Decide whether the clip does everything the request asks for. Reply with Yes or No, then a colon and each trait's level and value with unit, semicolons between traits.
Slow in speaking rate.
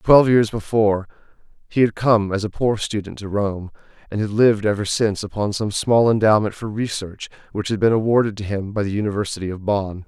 No: average, 200 wpm